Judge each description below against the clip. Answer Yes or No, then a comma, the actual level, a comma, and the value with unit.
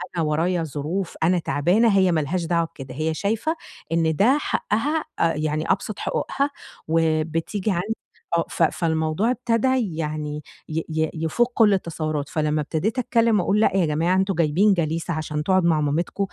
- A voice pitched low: No, medium, 165 Hz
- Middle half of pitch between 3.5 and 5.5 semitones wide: Yes, average, 4.2 semitones